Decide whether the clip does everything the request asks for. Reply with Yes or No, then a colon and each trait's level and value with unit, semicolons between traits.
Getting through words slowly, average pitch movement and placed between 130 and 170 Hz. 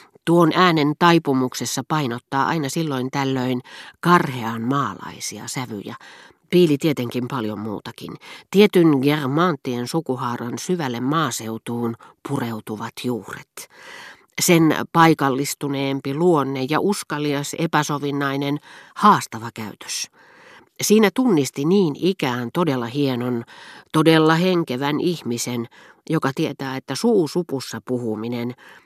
Yes: slow, 90 wpm; average, 4.7 semitones; medium, 140 Hz